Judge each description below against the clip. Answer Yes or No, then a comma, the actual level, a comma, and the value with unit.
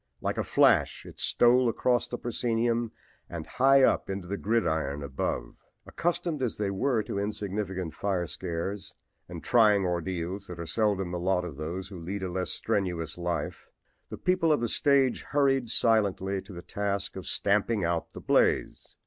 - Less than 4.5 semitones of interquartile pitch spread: No, average, 4.8 semitones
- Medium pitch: No, low, 100 Hz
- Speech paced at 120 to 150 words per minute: No, average, 170 wpm